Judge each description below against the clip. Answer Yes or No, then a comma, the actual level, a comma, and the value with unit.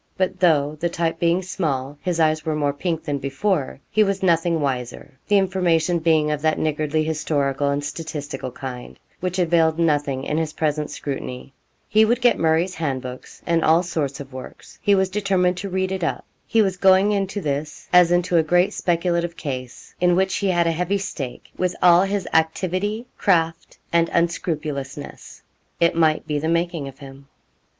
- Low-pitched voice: No, medium, 165 Hz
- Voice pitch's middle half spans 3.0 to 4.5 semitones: Yes, average, 3.7 semitones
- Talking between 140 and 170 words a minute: No, average, 180 wpm